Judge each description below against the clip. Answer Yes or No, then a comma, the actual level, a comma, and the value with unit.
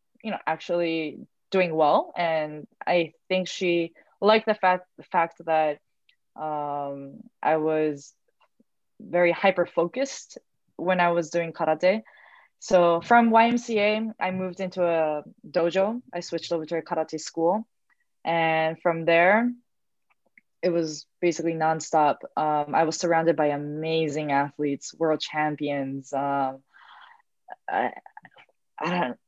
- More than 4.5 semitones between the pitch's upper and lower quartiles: No, average, 3.2 semitones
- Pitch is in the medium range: Yes, medium, 170 Hz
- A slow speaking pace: Yes, slow, 125 wpm